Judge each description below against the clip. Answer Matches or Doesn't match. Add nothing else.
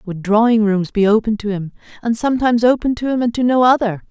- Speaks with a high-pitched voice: Matches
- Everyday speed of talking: Doesn't match